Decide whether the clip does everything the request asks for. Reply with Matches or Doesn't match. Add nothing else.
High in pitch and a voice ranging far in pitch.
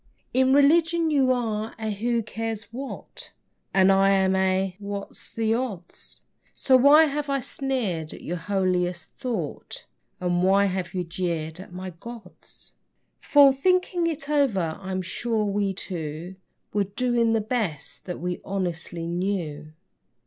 Matches